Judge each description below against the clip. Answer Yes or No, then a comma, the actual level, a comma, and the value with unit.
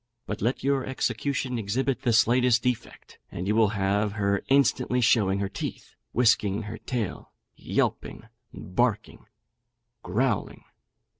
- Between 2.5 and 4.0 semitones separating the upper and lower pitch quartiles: Yes, average, 3.3 semitones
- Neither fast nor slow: No, slow, 130 wpm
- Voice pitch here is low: Yes, low, 115 Hz